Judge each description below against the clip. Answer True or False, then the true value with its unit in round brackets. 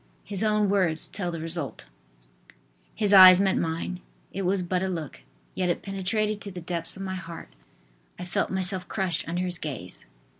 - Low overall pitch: False (185 Hz)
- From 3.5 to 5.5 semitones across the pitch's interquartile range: False (2.4 semitones)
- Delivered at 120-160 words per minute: False (180 wpm)